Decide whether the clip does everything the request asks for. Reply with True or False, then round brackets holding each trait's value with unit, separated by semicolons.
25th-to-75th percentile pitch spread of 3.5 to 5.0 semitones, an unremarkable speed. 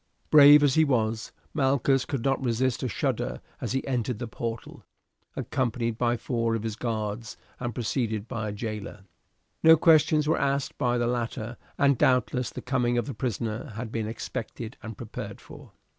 False (2.9 semitones; 175 wpm)